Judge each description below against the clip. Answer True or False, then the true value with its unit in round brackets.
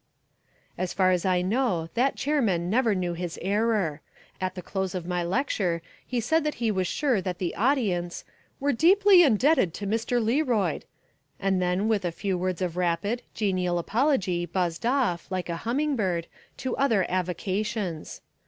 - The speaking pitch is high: True (195 Hz)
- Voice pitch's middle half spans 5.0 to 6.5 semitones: True (5.3 semitones)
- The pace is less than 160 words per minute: False (165 wpm)